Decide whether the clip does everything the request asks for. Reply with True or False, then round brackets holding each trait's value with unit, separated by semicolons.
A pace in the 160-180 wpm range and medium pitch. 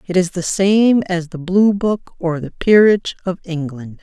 False (195 wpm; 180 Hz)